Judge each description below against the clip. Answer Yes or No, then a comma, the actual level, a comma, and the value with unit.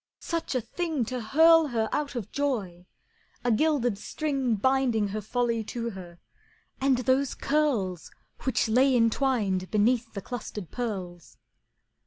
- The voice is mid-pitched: No, high, 240 Hz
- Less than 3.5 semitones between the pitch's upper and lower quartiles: No, average, 4.4 semitones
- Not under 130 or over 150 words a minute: Yes, slow, 135 wpm